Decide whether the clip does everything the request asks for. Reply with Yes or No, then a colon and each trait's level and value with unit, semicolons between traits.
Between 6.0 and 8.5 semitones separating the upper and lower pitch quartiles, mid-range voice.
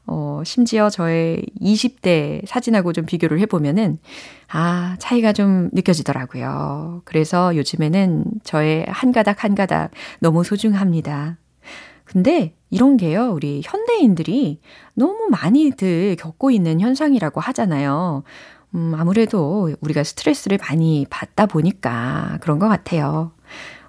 No: average, 5.1 semitones; medium, 180 Hz